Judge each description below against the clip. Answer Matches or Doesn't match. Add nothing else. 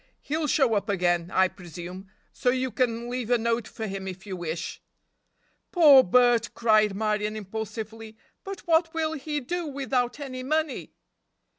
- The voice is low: Doesn't match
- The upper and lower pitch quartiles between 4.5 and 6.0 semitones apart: Matches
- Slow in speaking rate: Doesn't match